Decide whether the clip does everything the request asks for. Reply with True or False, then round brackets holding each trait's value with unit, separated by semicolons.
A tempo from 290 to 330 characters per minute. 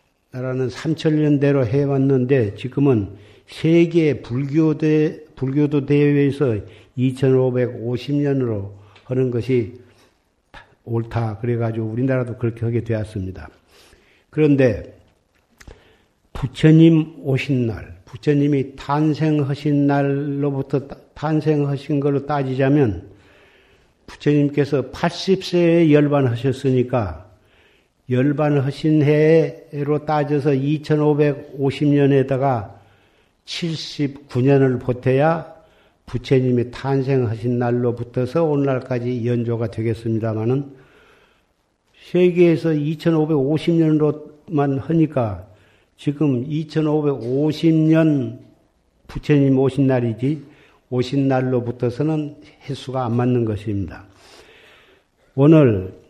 False (200 characters per minute)